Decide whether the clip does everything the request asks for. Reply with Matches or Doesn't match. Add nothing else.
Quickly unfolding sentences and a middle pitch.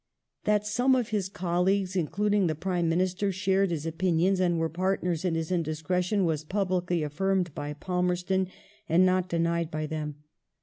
Doesn't match